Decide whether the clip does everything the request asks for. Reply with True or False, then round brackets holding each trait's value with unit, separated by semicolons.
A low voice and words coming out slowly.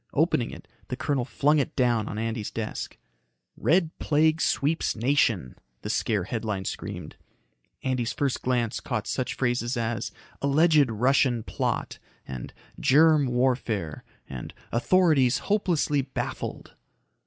True (125 Hz; 120 wpm)